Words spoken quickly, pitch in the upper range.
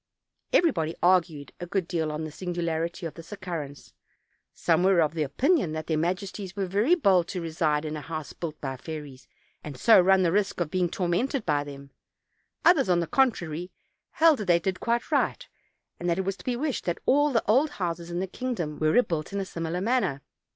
No: fast, 210 wpm; medium, 175 Hz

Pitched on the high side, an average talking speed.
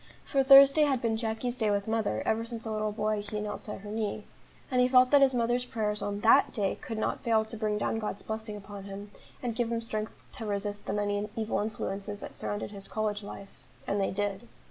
No: high, 215 Hz; fast, 230 wpm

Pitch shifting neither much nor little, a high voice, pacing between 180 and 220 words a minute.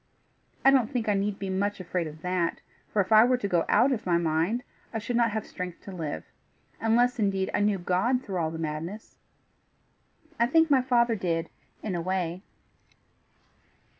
Yes: average, 5.0 semitones; high, 200 Hz; average, 190 wpm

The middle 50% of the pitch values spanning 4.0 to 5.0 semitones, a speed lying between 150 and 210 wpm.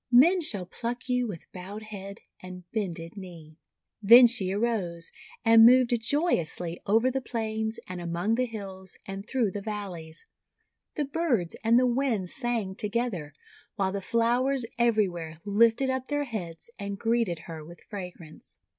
Yes: average, 4.7 semitones; average, 155 wpm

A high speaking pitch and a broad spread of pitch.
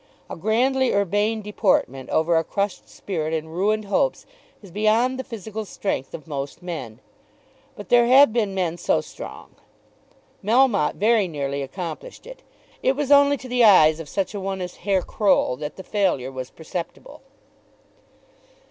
Yes: high, 200 Hz; wide, 5.8 semitones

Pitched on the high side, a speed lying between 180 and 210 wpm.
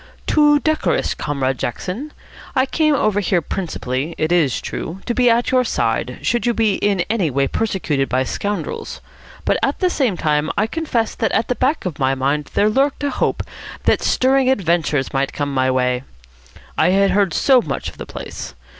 Yes: high, 195 Hz; average, 190 wpm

